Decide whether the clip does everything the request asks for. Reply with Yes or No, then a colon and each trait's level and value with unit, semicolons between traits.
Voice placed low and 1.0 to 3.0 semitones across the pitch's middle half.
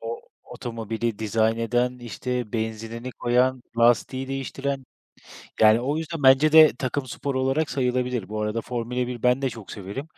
Yes: low, 125 Hz; narrow, 2.6 semitones